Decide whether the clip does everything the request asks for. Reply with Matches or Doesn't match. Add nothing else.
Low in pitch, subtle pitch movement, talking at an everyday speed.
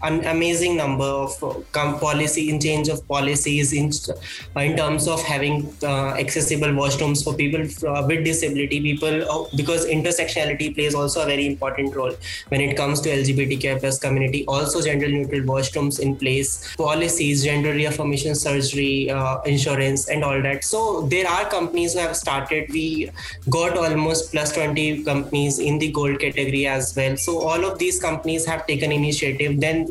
Doesn't match